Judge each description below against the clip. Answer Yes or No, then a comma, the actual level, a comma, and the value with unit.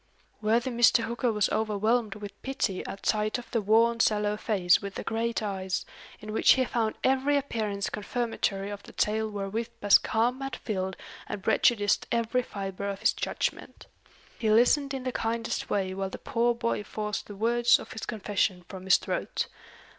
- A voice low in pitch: No, high, 220 Hz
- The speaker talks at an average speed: Yes, average, 175 wpm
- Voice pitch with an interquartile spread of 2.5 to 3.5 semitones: Yes, average, 2.8 semitones